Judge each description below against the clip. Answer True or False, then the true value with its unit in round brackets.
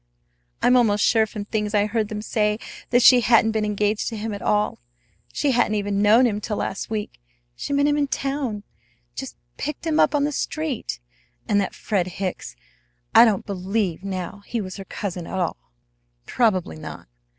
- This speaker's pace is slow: False (185 wpm)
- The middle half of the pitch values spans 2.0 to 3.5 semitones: True (3.1 semitones)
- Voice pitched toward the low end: False (210 Hz)